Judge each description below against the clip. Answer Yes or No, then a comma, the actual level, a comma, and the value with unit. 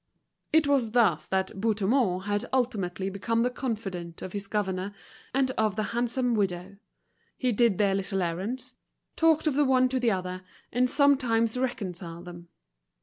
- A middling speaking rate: Yes, average, 155 wpm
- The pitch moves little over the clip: No, average, 4.9 semitones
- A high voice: Yes, high, 215 Hz